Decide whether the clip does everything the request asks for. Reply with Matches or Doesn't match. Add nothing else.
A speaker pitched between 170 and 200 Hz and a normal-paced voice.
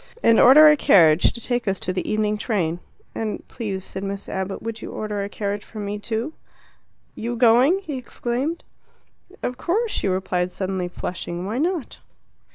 Doesn't match